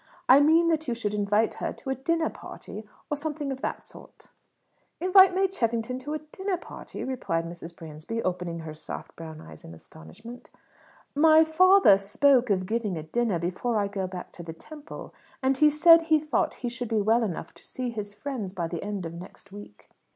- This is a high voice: Yes, high, 230 Hz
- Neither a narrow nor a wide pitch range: No, wide, 8.3 semitones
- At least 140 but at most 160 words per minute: No, average, 200 wpm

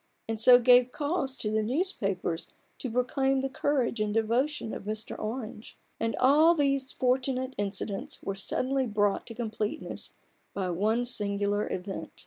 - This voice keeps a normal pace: Yes, average, 150 wpm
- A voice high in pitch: Yes, high, 235 Hz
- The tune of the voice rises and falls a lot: No, average, 4.1 semitones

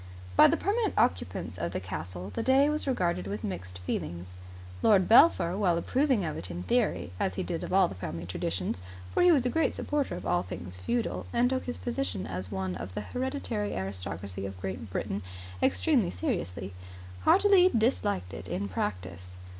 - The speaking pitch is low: Yes, very low, 95 Hz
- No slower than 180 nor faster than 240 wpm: Yes, average, 185 wpm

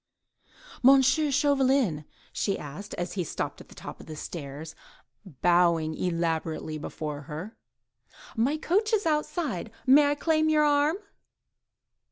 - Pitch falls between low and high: No, high, 220 Hz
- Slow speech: Yes, slow, 130 wpm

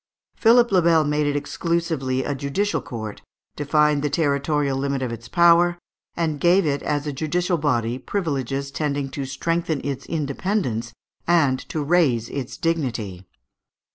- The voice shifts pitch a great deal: No, average, 3.9 semitones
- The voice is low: No, medium, 145 Hz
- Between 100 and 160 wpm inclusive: Yes, average, 145 wpm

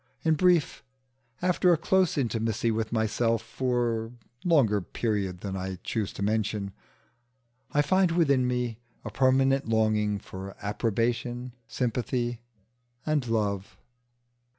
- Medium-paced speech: No, slow, 120 wpm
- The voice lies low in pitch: Yes, low, 115 Hz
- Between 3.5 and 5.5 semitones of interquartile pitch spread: Yes, average, 3.8 semitones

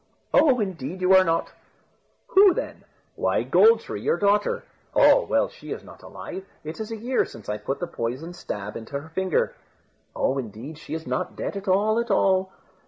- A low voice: No, medium, 185 Hz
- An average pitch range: No, wide, 7.1 semitones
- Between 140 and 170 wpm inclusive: No, average, 190 wpm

